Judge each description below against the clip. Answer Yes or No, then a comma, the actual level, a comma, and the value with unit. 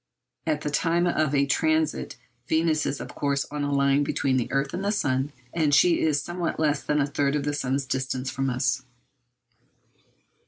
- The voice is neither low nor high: Yes, medium, 145 Hz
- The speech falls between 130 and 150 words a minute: No, average, 195 wpm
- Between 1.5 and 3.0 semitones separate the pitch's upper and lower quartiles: Yes, narrow, 2.4 semitones